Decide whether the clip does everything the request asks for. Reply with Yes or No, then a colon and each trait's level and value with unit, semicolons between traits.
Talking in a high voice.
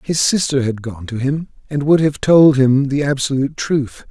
No: medium, 140 Hz